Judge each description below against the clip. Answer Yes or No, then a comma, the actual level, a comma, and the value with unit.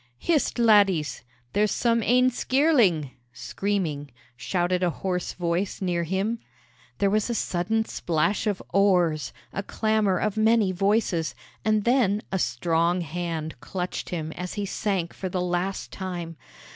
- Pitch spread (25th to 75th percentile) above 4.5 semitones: No, average, 3.7 semitones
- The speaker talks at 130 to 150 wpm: Yes, average, 140 wpm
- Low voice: No, high, 190 Hz